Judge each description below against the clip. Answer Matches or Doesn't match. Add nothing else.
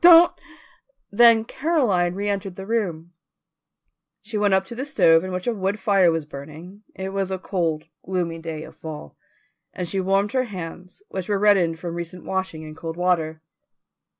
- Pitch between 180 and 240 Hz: Matches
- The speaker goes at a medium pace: Matches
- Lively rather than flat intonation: Doesn't match